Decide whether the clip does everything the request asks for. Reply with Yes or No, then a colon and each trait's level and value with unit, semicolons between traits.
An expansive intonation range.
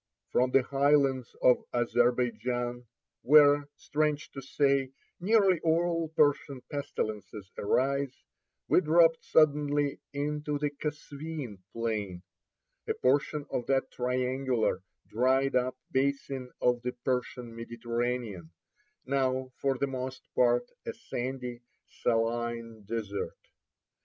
No: average, 3.0 semitones